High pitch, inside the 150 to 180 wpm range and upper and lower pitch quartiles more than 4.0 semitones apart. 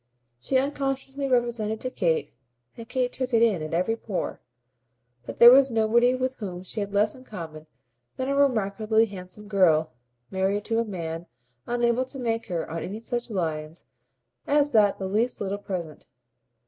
Yes: high, 220 Hz; average, 170 wpm; average, 4.9 semitones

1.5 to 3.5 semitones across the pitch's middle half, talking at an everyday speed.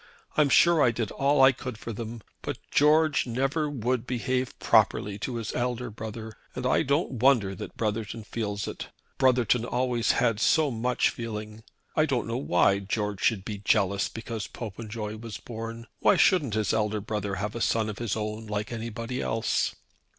Yes: average, 3.0 semitones; average, 175 wpm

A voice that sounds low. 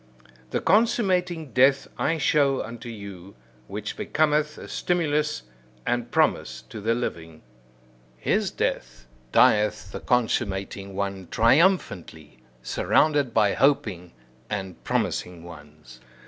Yes: low, 115 Hz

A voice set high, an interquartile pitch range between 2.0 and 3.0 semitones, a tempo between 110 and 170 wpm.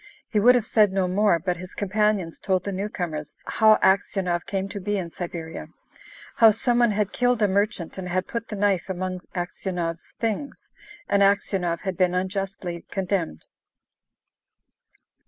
Yes: high, 195 Hz; average, 2.7 semitones; average, 155 wpm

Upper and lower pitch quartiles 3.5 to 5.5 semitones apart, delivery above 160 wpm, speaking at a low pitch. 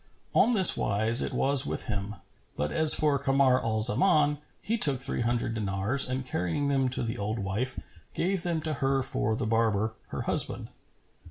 Yes: average, 4.5 semitones; average, 180 wpm; low, 130 Hz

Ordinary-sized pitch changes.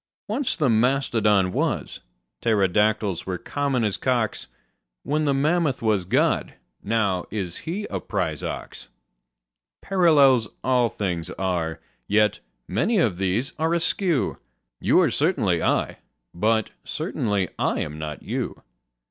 No: wide, 6.6 semitones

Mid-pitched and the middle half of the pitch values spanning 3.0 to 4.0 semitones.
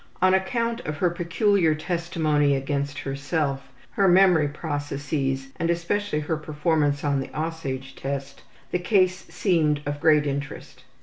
Yes: medium, 155 Hz; average, 3.4 semitones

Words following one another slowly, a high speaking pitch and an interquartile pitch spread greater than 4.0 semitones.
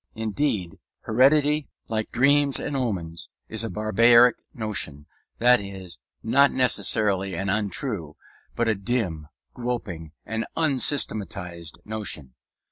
No: slow, 110 wpm; low, 110 Hz; average, 4.8 semitones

